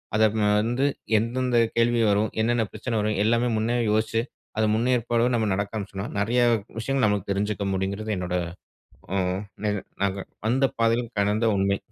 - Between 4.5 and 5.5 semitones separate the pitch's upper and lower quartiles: No, average, 2.7 semitones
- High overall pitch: No, low, 110 Hz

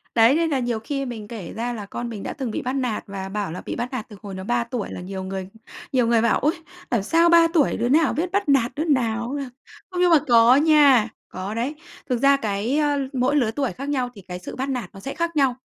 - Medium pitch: No, high, 245 Hz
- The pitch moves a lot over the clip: No, average, 4.5 semitones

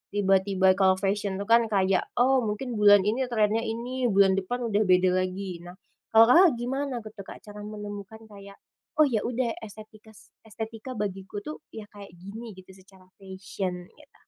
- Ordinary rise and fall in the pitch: Yes, average, 3.1 semitones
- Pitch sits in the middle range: No, high, 205 Hz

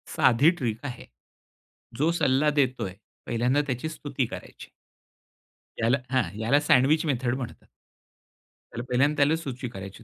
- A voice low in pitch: Yes, low, 130 Hz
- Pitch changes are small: No, average, 3.3 semitones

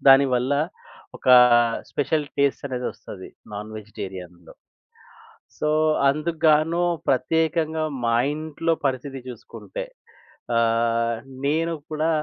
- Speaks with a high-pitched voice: No, medium, 140 Hz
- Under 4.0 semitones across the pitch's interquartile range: No, average, 5.1 semitones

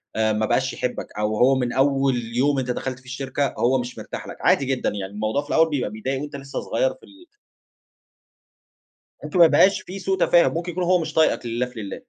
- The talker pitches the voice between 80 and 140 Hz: Yes, low, 135 Hz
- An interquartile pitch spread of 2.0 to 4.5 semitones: No, average, 4.9 semitones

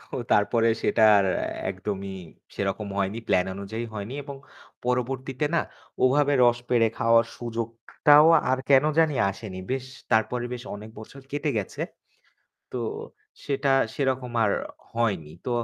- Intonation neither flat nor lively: Yes, average, 4.1 semitones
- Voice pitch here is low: Yes, low, 115 Hz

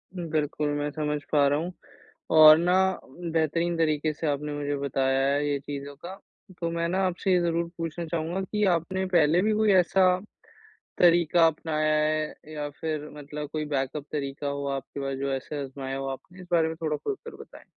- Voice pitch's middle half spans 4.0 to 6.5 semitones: No, average, 3.0 semitones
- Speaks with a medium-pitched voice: Yes, medium, 155 Hz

